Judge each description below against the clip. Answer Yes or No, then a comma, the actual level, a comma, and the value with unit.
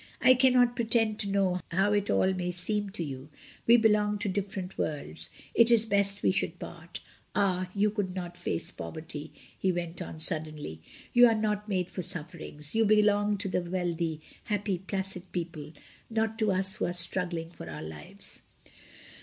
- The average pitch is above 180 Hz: Yes, high, 190 Hz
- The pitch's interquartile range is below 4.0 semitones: Yes, average, 3.6 semitones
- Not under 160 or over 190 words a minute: Yes, average, 175 wpm